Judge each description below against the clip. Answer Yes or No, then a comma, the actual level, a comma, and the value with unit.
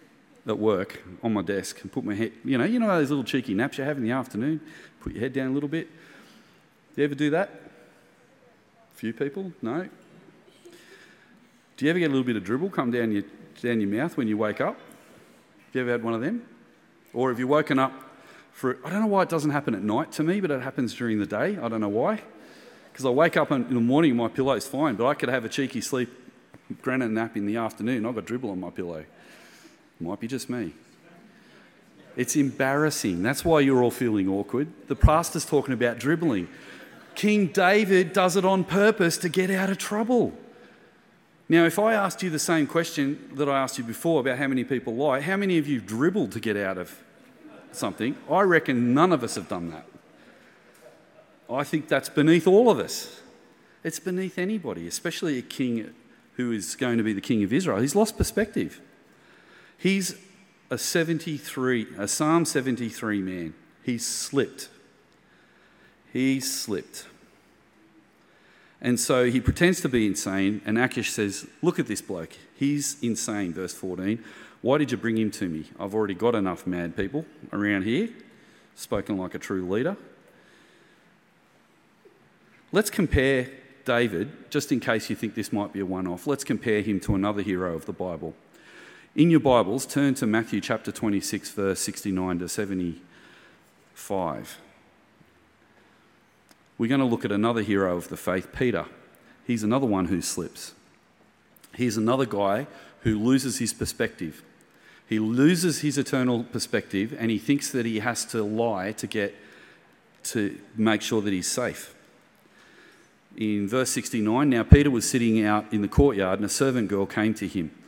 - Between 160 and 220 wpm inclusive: Yes, average, 180 wpm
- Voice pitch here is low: Yes, low, 125 Hz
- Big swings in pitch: Yes, wide, 6.2 semitones